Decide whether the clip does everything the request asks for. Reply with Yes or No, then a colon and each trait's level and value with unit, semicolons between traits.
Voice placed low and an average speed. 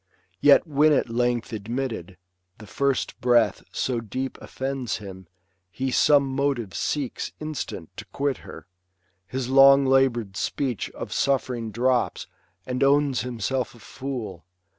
No: low, 130 Hz; slow, 130 wpm